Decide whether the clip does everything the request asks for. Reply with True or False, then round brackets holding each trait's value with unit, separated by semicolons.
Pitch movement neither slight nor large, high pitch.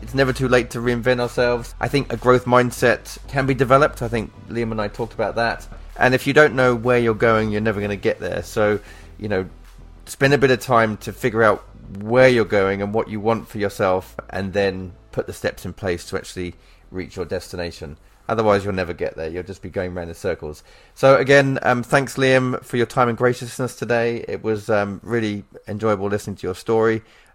False (4.1 semitones; 110 Hz)